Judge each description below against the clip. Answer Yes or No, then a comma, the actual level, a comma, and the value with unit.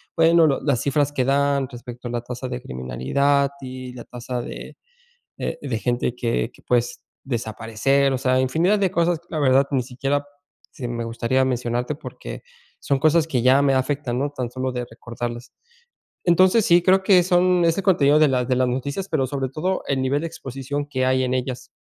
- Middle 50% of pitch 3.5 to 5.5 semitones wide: No, average, 2.9 semitones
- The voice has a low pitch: Yes, low, 130 Hz